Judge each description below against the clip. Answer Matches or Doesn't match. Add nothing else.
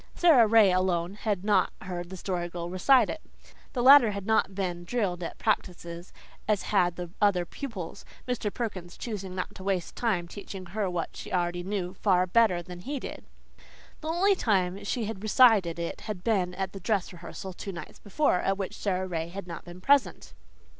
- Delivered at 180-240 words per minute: Matches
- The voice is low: Doesn't match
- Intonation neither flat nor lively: Matches